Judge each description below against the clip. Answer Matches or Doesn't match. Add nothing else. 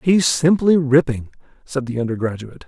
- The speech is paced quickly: Doesn't match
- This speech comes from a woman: Doesn't match